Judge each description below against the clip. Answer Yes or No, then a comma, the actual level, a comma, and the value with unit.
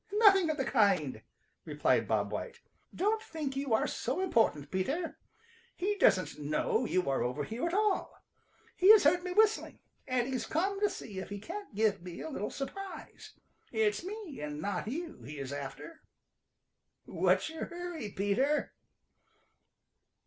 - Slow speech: No, average, 155 wpm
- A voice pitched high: Yes, very high, 270 Hz